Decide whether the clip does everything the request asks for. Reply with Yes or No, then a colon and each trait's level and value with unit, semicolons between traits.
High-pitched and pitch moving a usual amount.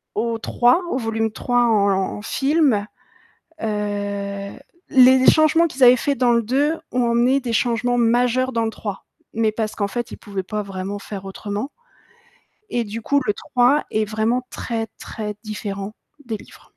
Yes: high, 225 Hz; average, 3.2 semitones